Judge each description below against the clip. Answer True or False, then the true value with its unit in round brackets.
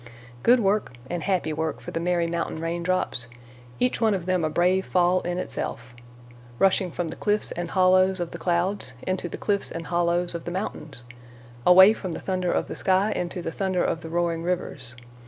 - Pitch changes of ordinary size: False (2.1 semitones)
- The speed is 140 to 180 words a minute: False (195 wpm)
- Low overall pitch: False (175 Hz)